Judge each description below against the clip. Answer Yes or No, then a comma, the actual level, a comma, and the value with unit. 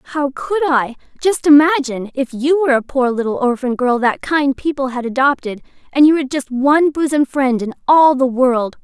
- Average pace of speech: Yes, average, 195 wpm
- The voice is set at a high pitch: Yes, very high, 270 Hz